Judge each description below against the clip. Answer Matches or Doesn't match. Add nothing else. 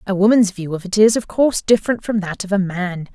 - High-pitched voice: Matches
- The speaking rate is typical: Doesn't match